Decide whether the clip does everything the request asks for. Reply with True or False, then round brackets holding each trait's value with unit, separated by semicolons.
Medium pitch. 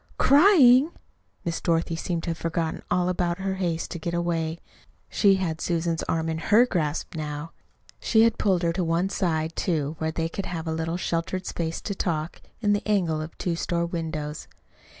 True (170 Hz)